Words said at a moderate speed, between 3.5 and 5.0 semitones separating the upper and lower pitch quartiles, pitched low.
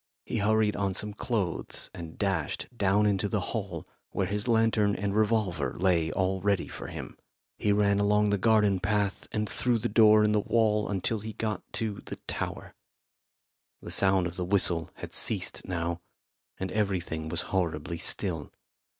No: average, 165 wpm; average, 2.7 semitones; low, 100 Hz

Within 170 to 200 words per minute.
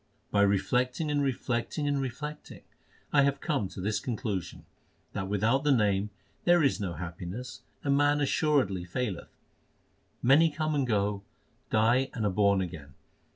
No: average, 150 wpm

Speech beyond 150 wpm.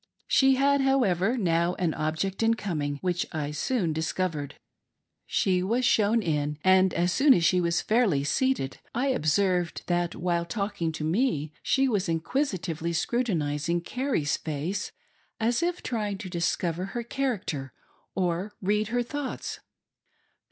No: average, 145 wpm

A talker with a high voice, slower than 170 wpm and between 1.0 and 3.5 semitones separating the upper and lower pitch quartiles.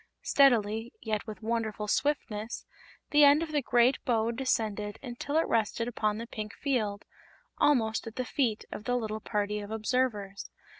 Yes: high, 225 Hz; average, 160 wpm; average, 3.1 semitones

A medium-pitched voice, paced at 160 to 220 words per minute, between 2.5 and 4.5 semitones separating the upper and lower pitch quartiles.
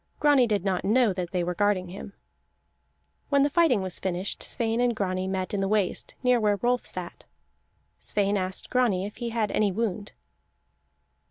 No: high, 205 Hz; average, 175 wpm; average, 3.9 semitones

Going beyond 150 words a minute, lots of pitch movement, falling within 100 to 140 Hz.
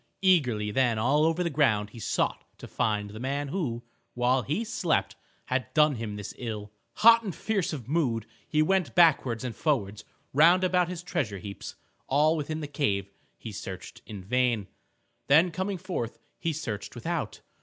Yes: average, 170 wpm; wide, 7.1 semitones; low, 135 Hz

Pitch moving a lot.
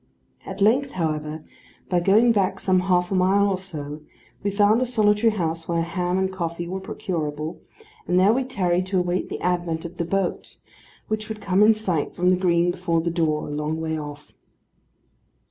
No: average, 3.1 semitones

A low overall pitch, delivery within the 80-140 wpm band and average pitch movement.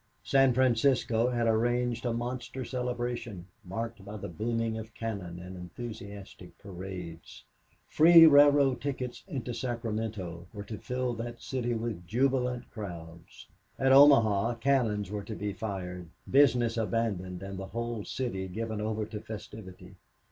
Yes: low, 115 Hz; slow, 135 wpm; average, 3.8 semitones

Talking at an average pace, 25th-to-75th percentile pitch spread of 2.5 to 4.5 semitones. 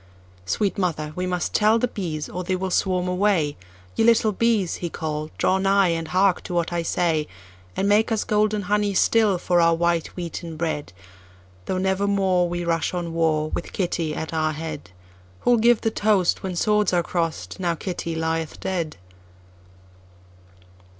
Yes: average, 150 wpm; average, 3.7 semitones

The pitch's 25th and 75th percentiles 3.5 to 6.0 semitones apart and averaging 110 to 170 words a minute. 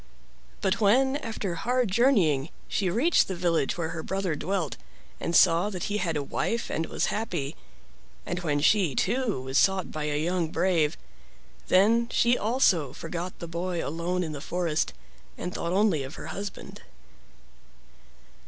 Yes: average, 4.4 semitones; average, 160 wpm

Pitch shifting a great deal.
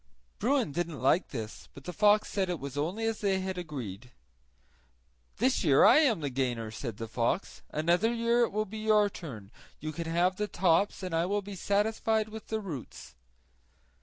Yes: wide, 6.9 semitones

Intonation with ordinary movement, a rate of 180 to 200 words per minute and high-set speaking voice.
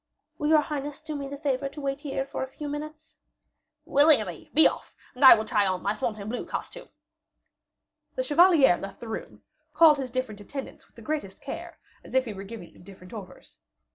No: wide, 5.8 semitones; average, 195 wpm; very high, 270 Hz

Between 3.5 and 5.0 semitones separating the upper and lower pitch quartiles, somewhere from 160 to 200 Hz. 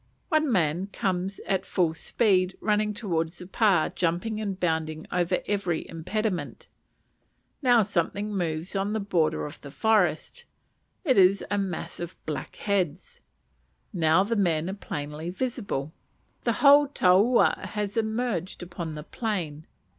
Yes: average, 4.3 semitones; high, 190 Hz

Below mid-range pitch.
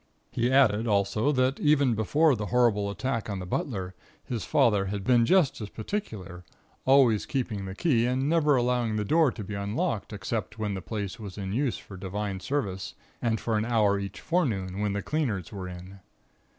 Yes: low, 110 Hz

